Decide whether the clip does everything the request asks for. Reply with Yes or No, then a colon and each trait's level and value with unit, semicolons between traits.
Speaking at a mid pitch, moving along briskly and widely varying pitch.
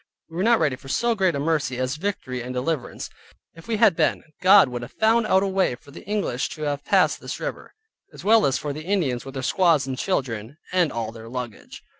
Yes: medium, 150 Hz; fast, 235 wpm; wide, 7.0 semitones